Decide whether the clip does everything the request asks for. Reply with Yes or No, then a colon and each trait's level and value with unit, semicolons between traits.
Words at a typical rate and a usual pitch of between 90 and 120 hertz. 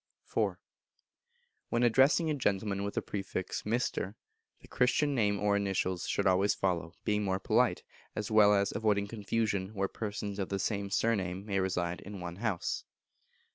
Yes: average, 160 wpm; low, 100 Hz